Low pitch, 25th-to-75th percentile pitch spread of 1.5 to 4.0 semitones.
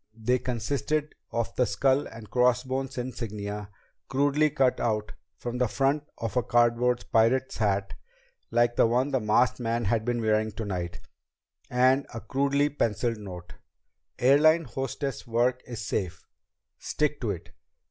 Yes: low, 120 Hz; average, 3.2 semitones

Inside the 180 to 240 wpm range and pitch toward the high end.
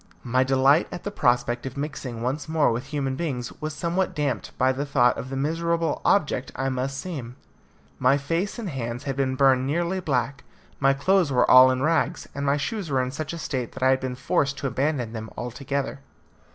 No: fast, 205 wpm; low, 135 Hz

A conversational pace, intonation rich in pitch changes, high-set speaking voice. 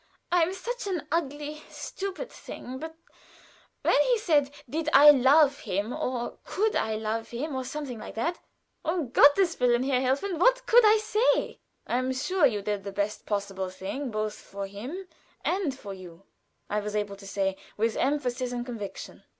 Yes: average, 175 wpm; wide, 7.3 semitones; very high, 260 Hz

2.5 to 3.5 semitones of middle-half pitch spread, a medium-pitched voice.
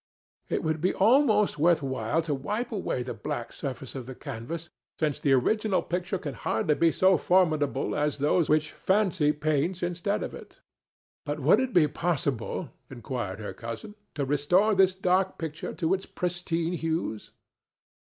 No: average, 4.7 semitones; medium, 160 Hz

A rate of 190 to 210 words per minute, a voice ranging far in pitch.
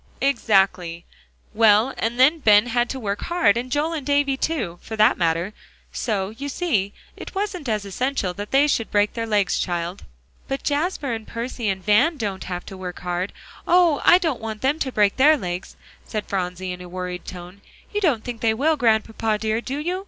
Yes: average, 195 wpm; wide, 6.2 semitones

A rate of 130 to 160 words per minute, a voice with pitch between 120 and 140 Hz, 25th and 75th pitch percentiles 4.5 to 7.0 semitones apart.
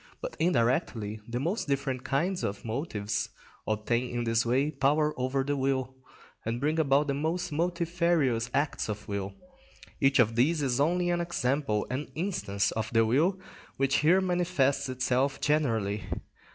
Yes: average, 150 wpm; low, 135 Hz; average, 5.0 semitones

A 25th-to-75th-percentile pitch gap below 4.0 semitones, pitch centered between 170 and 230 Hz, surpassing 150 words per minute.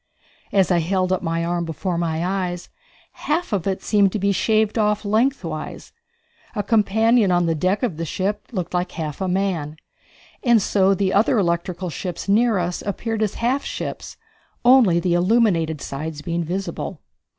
Yes: average, 3.6 semitones; medium, 185 Hz; average, 165 wpm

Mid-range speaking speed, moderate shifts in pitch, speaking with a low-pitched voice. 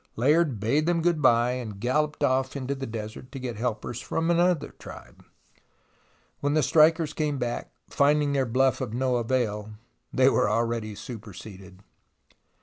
Yes: average, 150 wpm; average, 4.4 semitones; low, 130 Hz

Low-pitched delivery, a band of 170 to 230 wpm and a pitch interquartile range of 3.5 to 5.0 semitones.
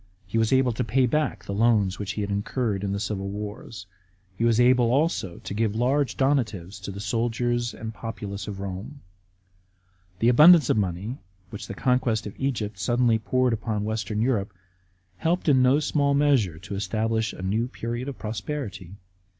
Yes: low, 110 Hz; average, 180 wpm; average, 3.9 semitones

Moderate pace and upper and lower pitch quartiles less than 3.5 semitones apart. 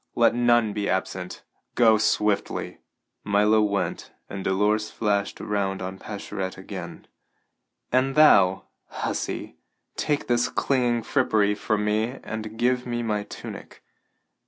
No: slow, 120 wpm; average, 2.9 semitones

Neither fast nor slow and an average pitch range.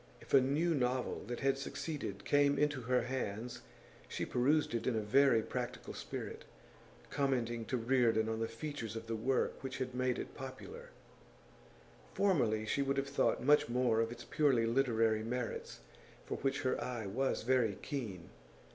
Yes: average, 165 wpm; average, 3.2 semitones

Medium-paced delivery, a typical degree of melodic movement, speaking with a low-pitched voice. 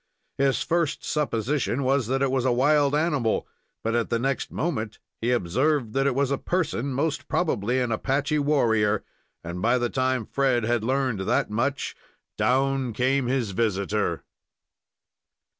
Yes: average, 150 wpm; average, 3.4 semitones; low, 130 Hz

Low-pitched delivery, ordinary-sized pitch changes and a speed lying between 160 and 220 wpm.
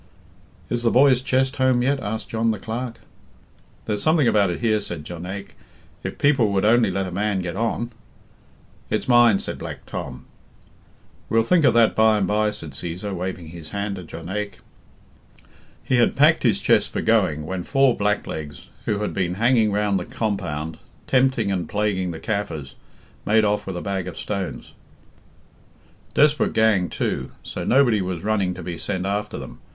Yes: low, 105 Hz; average, 4.1 semitones; average, 175 wpm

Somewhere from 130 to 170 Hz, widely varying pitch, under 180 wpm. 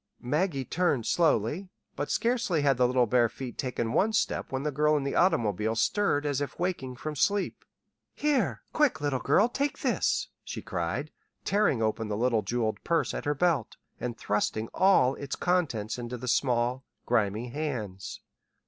Yes: low, 135 Hz; wide, 6.4 semitones; average, 165 wpm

